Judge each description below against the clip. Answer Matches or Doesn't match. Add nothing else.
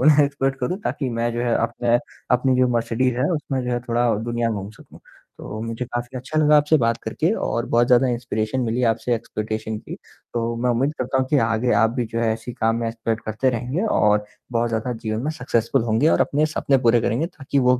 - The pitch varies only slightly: Matches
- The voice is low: Matches